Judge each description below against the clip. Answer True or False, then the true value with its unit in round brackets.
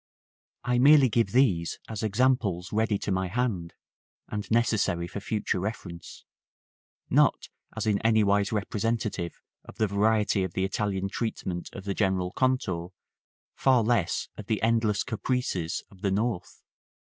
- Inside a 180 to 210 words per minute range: False (150 wpm)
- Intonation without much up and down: False (3.3 semitones)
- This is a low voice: True (105 Hz)